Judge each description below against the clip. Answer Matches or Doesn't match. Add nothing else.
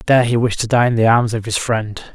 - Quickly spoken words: Matches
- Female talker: Doesn't match